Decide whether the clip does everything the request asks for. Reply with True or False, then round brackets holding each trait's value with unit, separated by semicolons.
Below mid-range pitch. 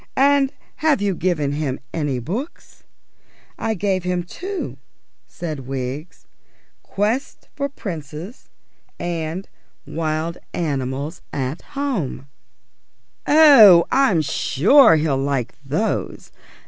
False (170 Hz)